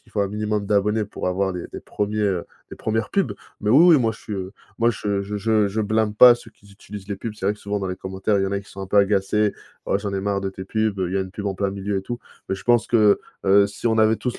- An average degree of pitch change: No, narrow, 1.9 semitones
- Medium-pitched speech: No, low, 100 Hz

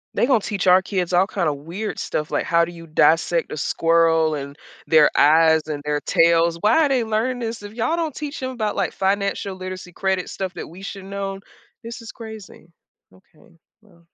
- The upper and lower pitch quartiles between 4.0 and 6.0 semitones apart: Yes, average, 4.6 semitones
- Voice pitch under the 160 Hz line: No, medium, 185 Hz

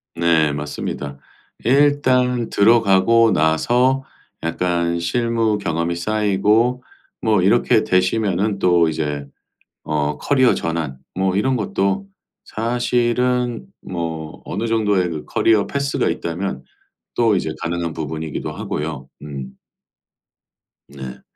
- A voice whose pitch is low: Yes, very low, 95 Hz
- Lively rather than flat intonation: Yes, wide, 6.2 semitones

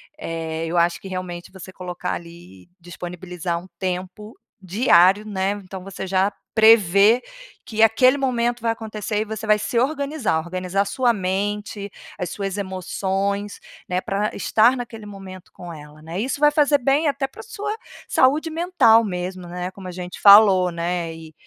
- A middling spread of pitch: Yes, average, 4.0 semitones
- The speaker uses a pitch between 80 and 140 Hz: No, high, 195 Hz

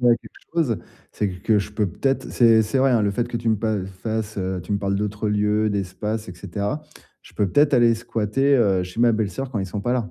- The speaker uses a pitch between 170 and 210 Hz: No, low, 105 Hz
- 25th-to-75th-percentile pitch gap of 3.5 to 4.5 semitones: No, average, 2.8 semitones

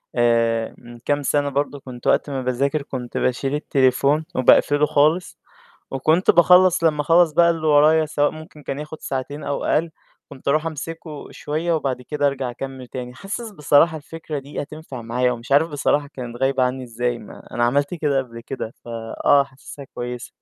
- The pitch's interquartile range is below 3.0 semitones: No, average, 3.4 semitones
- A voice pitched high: No, medium, 140 Hz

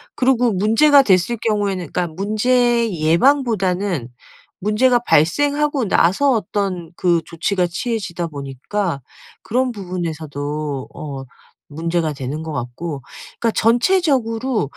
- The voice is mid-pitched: No, high, 195 Hz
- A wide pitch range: Yes, wide, 6.8 semitones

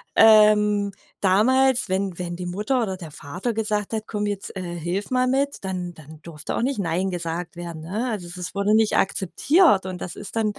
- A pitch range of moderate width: Yes, average, 3.6 semitones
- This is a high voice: Yes, high, 195 Hz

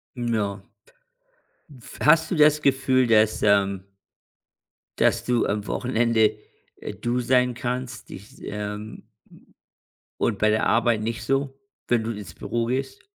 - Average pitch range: Yes, average, 3.0 semitones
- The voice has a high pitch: No, low, 115 Hz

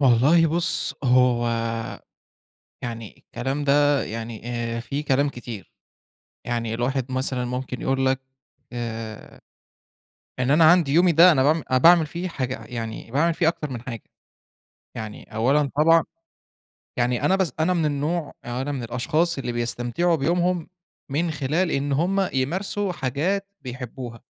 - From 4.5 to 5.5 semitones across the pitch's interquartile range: Yes, average, 5.2 semitones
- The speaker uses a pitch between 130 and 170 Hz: Yes, low, 135 Hz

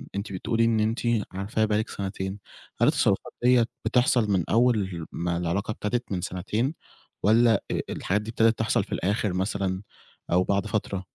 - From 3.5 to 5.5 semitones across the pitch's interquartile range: No, average, 2.9 semitones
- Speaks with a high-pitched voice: No, low, 105 Hz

